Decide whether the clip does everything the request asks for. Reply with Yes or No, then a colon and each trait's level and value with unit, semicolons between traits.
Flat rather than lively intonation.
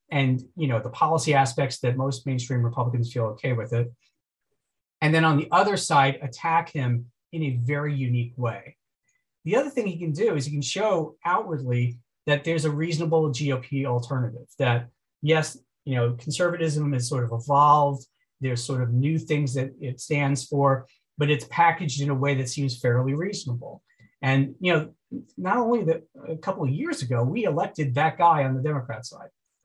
No: average, 3.7 semitones